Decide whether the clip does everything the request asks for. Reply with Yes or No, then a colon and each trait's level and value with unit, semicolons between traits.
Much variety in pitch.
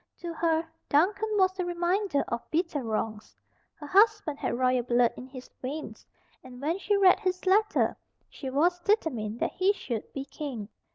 Yes: wide, 6.7 semitones